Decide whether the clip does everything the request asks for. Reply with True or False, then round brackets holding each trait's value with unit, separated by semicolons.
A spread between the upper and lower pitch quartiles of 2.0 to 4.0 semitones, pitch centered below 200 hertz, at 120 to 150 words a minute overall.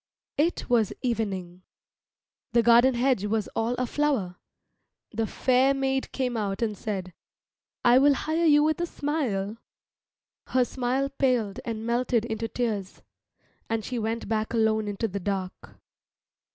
False (3.7 semitones; 230 Hz; 140 wpm)